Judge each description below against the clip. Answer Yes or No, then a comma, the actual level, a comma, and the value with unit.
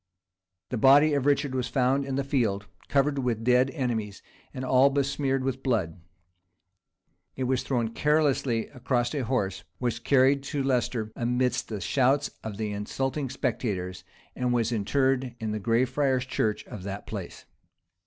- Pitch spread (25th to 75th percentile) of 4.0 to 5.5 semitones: No, average, 3.3 semitones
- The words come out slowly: No, average, 155 wpm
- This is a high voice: No, low, 125 Hz